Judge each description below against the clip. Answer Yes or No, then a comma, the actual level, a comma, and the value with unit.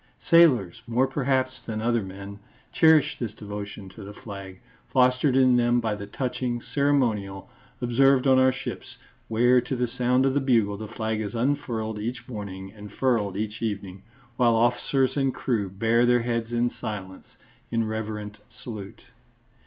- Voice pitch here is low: Yes, low, 115 Hz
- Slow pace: No, average, 160 wpm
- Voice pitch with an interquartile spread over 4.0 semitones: No, average, 3.6 semitones